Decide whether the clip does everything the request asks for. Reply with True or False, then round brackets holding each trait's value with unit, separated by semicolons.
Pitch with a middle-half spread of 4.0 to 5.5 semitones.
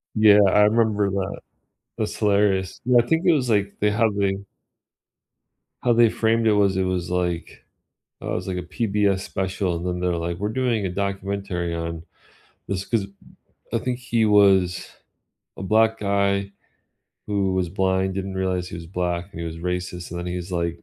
False (2.7 semitones)